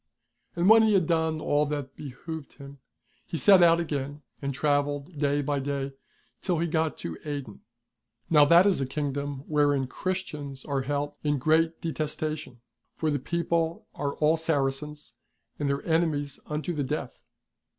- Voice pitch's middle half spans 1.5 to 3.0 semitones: Yes, narrow, 2.4 semitones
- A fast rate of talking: No, average, 160 wpm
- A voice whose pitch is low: No, medium, 150 Hz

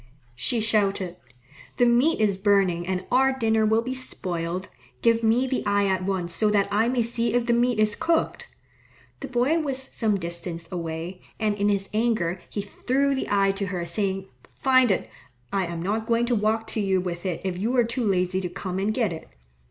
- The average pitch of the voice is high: Yes, high, 205 Hz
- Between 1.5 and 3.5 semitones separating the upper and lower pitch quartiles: No, average, 4.2 semitones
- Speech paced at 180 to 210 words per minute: Yes, fast, 205 wpm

